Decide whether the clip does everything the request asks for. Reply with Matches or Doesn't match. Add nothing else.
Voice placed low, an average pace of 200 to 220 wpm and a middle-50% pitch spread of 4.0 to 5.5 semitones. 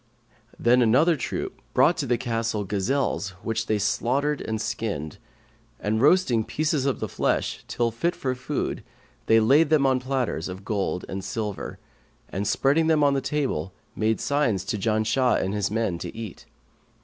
Doesn't match